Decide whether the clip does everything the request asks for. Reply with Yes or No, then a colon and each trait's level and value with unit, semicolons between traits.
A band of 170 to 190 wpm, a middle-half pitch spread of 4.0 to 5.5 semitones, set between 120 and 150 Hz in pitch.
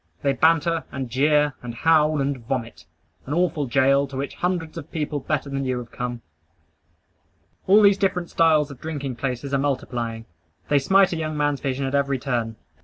No: average, 180 wpm; average, 3.2 semitones; medium, 140 Hz